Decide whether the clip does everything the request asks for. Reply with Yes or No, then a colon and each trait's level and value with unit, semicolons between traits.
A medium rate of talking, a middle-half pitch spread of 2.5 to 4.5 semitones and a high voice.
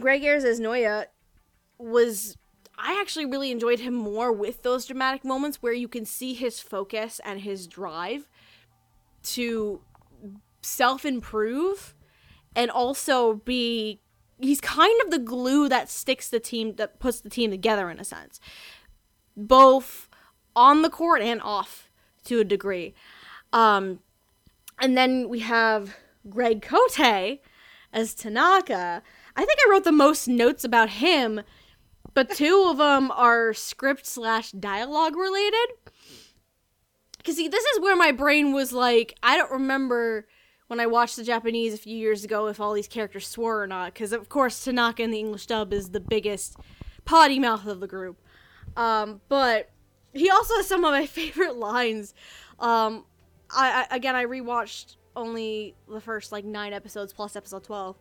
Yes: average, 155 wpm; average, 4.0 semitones; high, 235 Hz